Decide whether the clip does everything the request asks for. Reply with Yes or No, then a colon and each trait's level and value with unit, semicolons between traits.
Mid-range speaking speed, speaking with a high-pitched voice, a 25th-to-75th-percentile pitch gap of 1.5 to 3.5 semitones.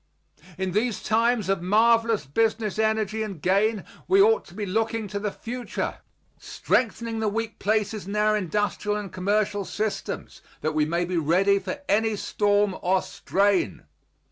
Yes: average, 155 wpm; high, 210 Hz; narrow, 2.5 semitones